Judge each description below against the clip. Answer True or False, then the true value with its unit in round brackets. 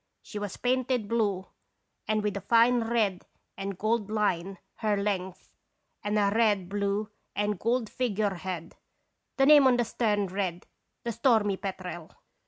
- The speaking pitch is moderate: False (205 Hz)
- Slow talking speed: False (145 wpm)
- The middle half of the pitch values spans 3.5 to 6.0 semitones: False (2.9 semitones)